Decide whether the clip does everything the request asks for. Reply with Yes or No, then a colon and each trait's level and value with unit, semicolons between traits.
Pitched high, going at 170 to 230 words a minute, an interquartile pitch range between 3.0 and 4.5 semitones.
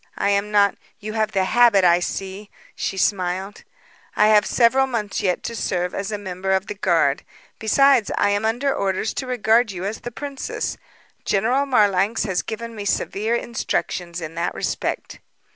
Yes: high, 205 Hz; average, 175 wpm; average, 3.3 semitones